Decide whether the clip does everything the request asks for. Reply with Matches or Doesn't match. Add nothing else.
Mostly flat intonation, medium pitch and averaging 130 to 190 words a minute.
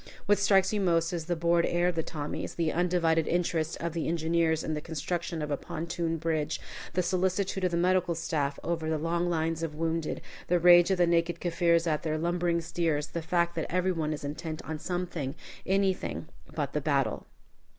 Doesn't match